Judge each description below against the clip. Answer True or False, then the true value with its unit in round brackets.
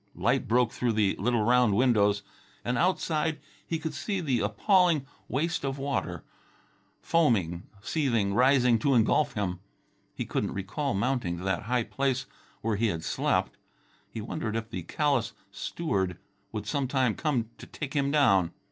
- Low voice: True (125 Hz)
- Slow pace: False (155 wpm)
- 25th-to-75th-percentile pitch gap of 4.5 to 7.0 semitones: True (5.4 semitones)